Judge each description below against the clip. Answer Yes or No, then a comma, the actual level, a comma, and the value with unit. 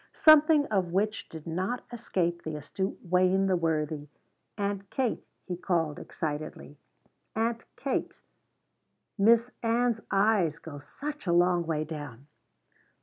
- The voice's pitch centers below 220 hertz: Yes, medium, 185 Hz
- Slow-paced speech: Yes, slow, 125 wpm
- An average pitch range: No, wide, 5.7 semitones